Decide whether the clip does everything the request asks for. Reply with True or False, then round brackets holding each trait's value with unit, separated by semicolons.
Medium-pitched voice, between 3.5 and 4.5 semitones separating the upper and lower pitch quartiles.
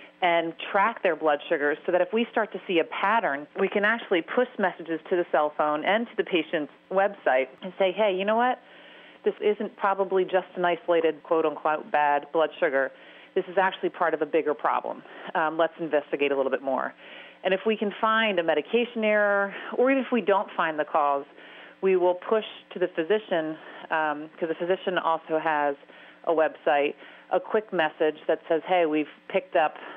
True (175 Hz; 4.2 semitones)